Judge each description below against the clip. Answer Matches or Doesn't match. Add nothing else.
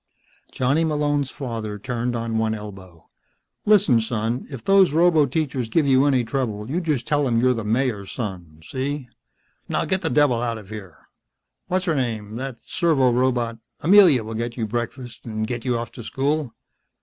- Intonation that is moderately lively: Matches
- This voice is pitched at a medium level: Doesn't match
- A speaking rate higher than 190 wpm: Doesn't match